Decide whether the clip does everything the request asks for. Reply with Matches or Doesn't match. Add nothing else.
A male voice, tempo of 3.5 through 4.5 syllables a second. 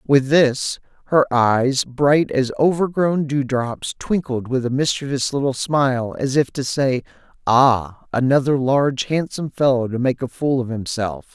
Matches